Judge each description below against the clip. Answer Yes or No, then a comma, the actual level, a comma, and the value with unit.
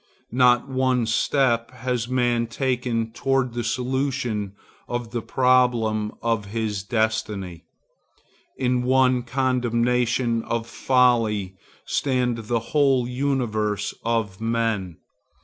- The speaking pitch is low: Yes, low, 120 Hz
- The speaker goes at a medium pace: No, slow, 100 wpm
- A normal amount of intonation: No, narrow, 2.2 semitones